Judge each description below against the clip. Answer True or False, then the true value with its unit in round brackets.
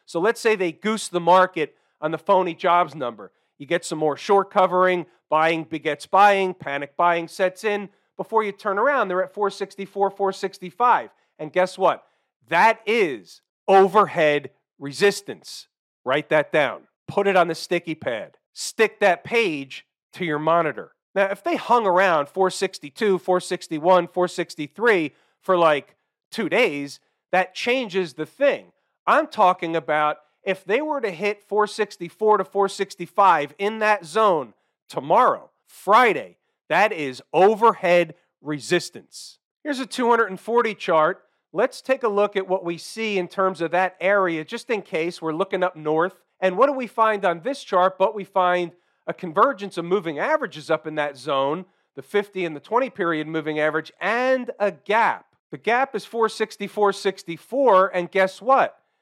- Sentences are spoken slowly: False (155 wpm)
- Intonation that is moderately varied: True (3.9 semitones)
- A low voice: False (190 Hz)